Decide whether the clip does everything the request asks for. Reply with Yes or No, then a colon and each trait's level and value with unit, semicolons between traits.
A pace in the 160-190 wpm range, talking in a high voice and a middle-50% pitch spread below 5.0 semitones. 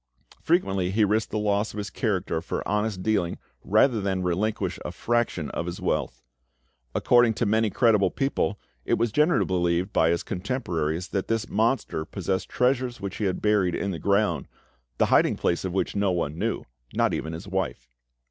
No: average, 180 wpm; low, 100 Hz; average, 3.5 semitones